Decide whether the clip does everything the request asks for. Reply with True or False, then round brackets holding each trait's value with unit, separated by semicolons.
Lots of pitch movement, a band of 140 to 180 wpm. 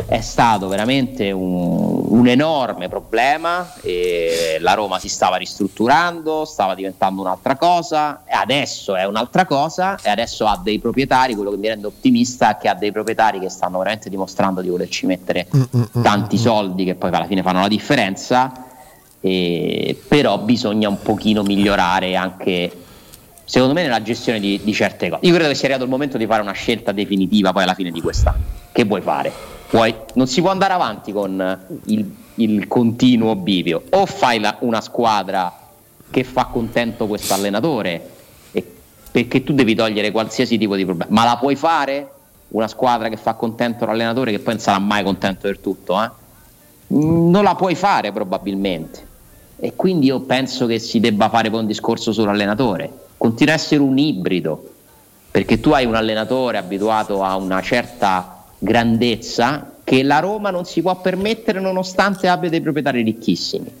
True (5.7 semitones; 170 wpm)